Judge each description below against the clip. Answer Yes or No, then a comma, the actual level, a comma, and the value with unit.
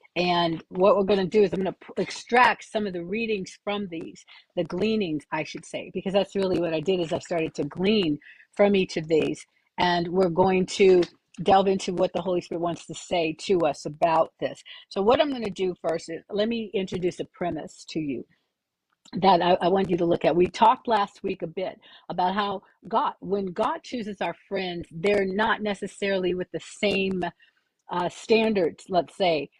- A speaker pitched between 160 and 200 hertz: Yes, high, 190 Hz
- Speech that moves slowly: No, fast, 205 wpm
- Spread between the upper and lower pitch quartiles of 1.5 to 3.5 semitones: Yes, average, 2.8 semitones